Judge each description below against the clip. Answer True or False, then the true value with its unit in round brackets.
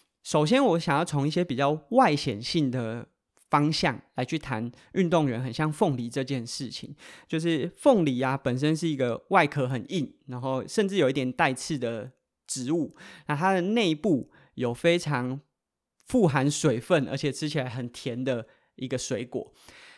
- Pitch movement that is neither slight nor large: True (4.5 semitones)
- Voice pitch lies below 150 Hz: True (140 Hz)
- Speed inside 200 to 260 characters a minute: True (240 characters per minute)